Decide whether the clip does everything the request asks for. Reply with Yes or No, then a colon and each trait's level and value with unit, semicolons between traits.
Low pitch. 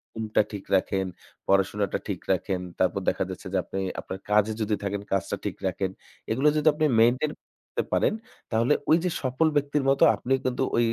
Yes: low, 110 Hz